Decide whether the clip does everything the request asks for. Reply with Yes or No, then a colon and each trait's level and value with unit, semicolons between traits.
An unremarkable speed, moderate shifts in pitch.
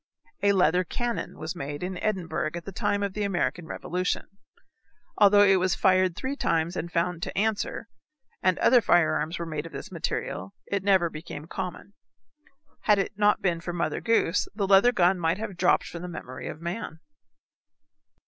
Yes: average, 175 wpm; average, 3.1 semitones